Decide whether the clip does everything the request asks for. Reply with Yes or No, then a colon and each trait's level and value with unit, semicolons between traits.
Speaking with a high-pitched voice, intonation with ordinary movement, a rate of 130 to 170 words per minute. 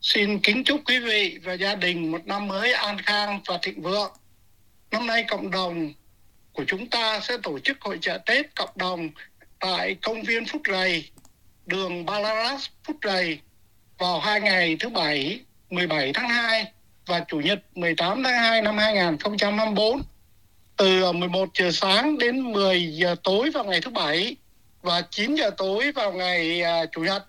Yes: high, 195 Hz; average, 3.9 semitones; slow, 165 wpm